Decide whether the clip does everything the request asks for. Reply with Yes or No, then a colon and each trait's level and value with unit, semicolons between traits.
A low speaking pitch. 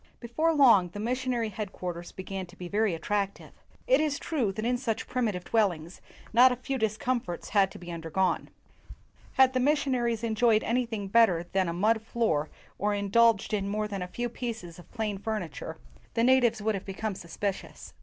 No: high, 215 Hz